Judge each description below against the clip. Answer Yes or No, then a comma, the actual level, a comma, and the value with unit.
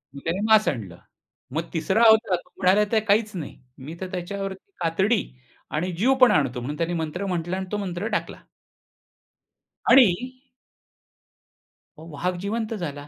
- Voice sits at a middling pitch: Yes, medium, 180 Hz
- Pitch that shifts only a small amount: No, average, 4.5 semitones